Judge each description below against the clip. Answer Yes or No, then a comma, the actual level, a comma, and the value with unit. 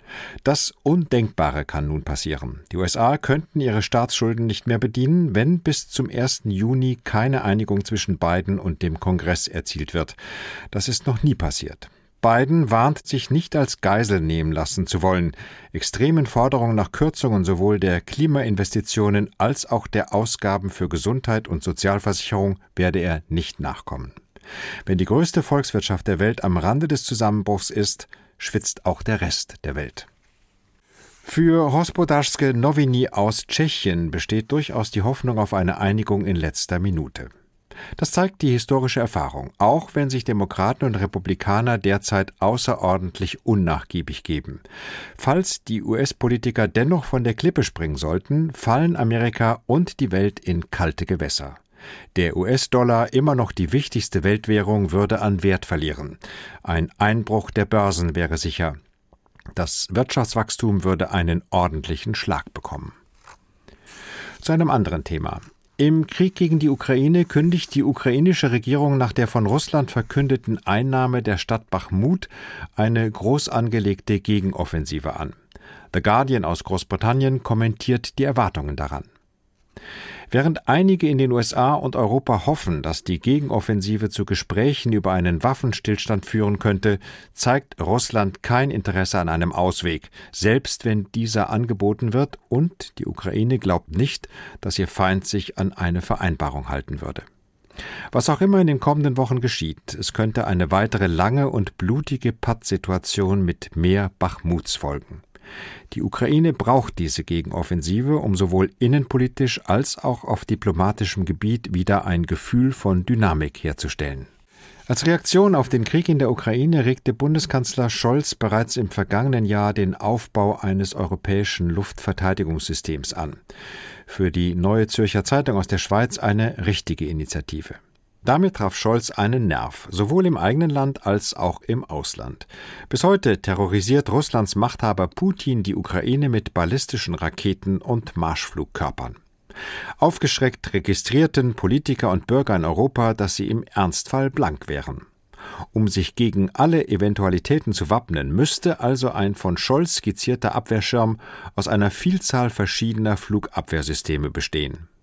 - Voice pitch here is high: No, low, 105 Hz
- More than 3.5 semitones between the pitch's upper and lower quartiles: Yes, wide, 5.6 semitones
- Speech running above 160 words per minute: No, average, 140 wpm